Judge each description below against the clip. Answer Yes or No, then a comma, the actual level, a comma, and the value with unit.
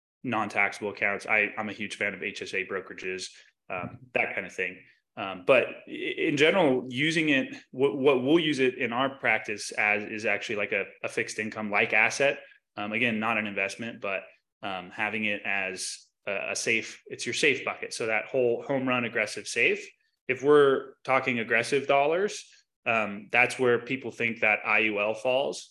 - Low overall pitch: Yes, low, 120 Hz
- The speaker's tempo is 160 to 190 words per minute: Yes, average, 180 wpm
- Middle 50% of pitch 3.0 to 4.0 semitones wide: No, average, 4.4 semitones